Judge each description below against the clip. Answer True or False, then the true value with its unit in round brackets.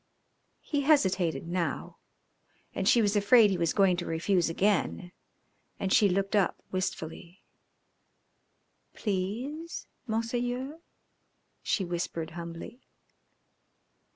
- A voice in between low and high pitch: False (195 Hz)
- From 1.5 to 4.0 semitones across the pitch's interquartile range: False (4.9 semitones)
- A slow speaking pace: True (100 wpm)